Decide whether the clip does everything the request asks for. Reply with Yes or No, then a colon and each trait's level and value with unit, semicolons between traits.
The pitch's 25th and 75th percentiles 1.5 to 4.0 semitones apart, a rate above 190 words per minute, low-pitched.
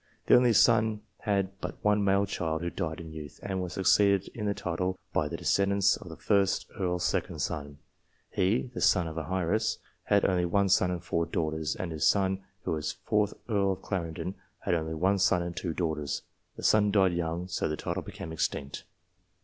Yes: average, 3.3 semitones; average, 200 wpm; very low, 95 Hz